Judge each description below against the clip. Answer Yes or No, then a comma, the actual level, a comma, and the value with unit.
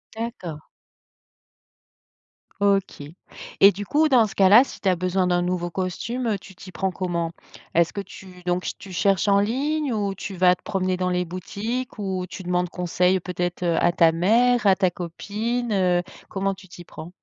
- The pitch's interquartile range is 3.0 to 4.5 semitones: No, narrow, 2.4 semitones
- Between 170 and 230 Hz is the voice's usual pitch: Yes, medium, 185 Hz